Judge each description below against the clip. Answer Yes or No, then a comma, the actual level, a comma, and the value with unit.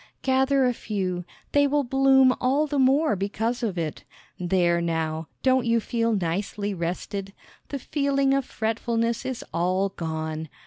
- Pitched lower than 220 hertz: No, high, 225 Hz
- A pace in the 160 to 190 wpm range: No, average, 145 wpm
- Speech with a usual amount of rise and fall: No, wide, 6.8 semitones